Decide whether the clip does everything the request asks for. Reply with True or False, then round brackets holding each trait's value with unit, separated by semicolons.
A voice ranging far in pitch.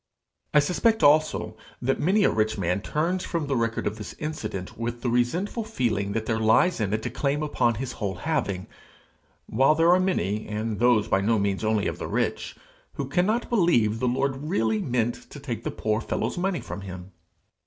True (6.1 semitones)